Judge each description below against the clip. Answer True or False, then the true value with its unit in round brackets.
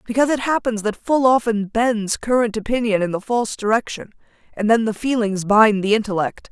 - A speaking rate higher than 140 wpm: True (185 wpm)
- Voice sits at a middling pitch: False (225 Hz)